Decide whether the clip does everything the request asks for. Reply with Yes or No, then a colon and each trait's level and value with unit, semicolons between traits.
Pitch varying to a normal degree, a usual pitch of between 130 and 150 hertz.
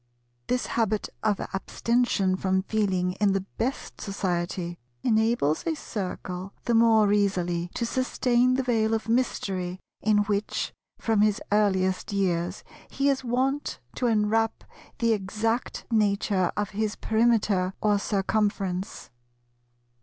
No: average, 3.2 semitones; high, 210 Hz